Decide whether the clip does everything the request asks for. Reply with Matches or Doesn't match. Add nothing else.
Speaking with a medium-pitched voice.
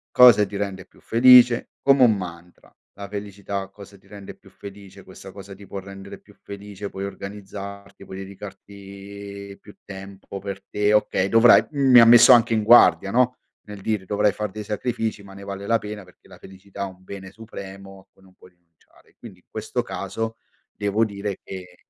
Doesn't match